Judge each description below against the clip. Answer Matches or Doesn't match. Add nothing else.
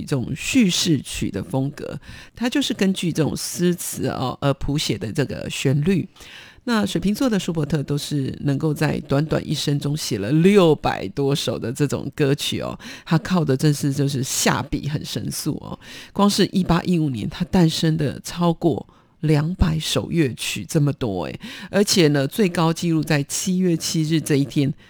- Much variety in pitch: Doesn't match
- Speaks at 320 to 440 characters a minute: Doesn't match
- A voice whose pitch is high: Doesn't match